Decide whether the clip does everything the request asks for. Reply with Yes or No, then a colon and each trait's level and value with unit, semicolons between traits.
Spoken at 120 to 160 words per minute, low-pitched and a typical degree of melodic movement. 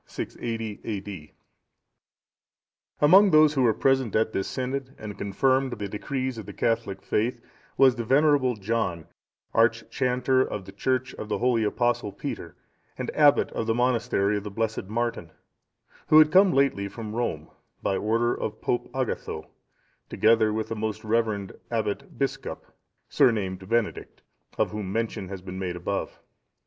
Yes: average, 150 wpm; low, 115 Hz; average, 3.9 semitones